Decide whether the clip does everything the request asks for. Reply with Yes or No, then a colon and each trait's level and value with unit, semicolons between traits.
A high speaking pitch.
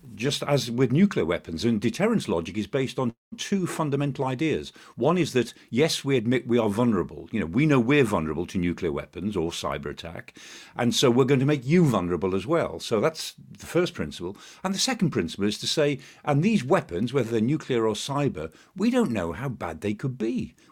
No: low, 135 Hz